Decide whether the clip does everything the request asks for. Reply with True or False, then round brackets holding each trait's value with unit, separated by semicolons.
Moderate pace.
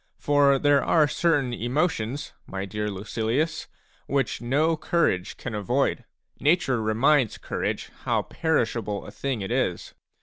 False (130 wpm)